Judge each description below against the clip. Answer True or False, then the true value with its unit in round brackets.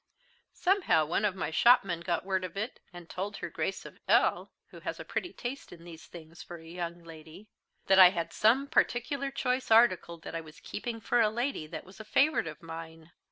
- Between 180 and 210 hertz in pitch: True (185 Hz)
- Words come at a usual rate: False (210 wpm)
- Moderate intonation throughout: False (6.1 semitones)